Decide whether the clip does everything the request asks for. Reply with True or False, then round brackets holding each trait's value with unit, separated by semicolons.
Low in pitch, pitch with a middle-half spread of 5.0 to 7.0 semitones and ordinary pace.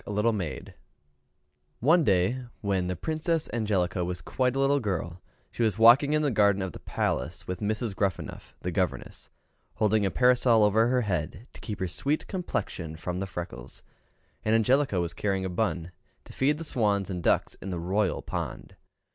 True (100 Hz; 5.5 semitones; 170 wpm)